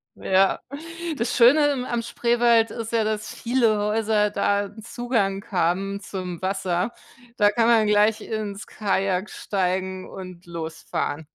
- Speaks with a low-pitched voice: No, high, 210 Hz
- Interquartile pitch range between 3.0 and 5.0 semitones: Yes, average, 3.3 semitones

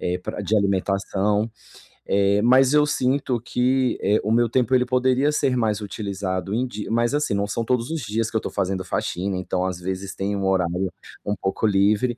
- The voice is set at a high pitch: No, low, 105 Hz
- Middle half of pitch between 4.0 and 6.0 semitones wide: Yes, average, 4.3 semitones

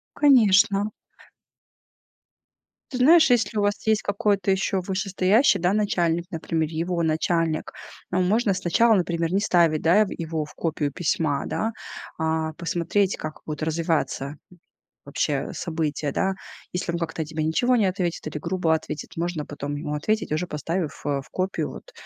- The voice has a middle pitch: Yes, medium, 175 Hz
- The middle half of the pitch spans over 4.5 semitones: No, average, 3.9 semitones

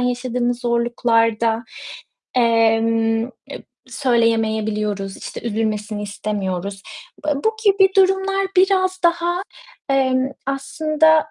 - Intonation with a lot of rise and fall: Yes, wide, 5.7 semitones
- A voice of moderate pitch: No, high, 240 Hz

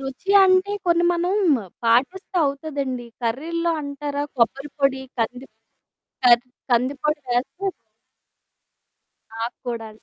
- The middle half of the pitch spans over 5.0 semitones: Yes, wide, 5.4 semitones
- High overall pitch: Yes, very high, 275 Hz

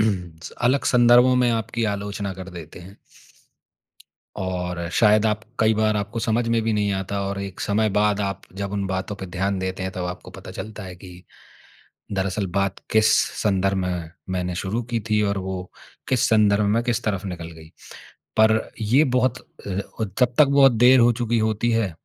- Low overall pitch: Yes, low, 100 Hz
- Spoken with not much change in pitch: No, average, 3.1 semitones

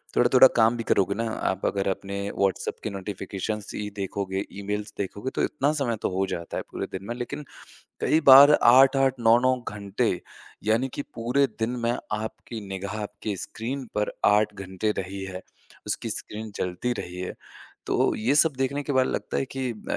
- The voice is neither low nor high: No, low, 110 Hz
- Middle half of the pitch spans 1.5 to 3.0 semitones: No, average, 4.3 semitones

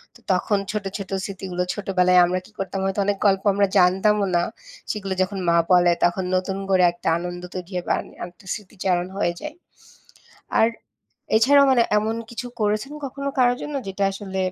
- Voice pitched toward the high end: Yes, high, 195 Hz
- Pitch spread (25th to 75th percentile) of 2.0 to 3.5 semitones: Yes, narrow, 2.6 semitones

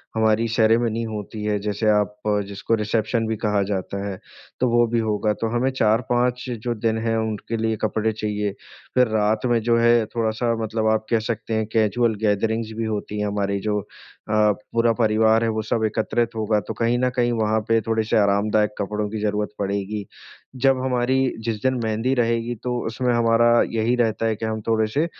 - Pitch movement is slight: Yes, narrow, 1.6 semitones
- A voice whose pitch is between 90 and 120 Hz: Yes, low, 110 Hz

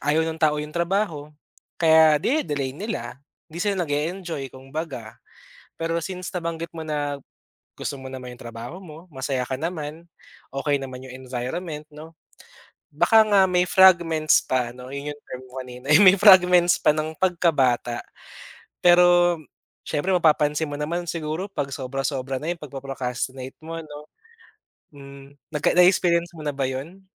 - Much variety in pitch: No, average, 4.3 semitones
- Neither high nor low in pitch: Yes, medium, 150 Hz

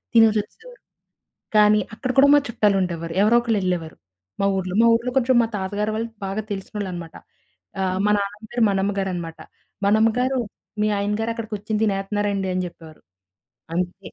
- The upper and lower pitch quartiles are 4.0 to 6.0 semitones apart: No, average, 2.9 semitones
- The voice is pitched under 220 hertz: Yes, high, 205 Hz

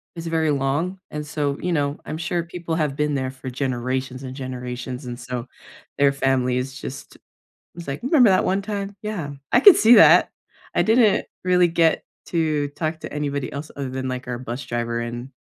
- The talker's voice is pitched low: No, medium, 145 Hz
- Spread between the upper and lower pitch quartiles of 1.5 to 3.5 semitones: No, average, 4.5 semitones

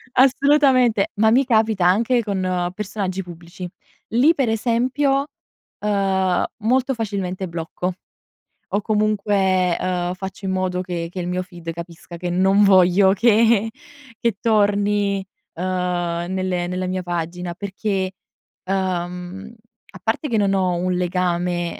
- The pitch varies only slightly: No, average, 3.1 semitones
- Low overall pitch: No, high, 190 Hz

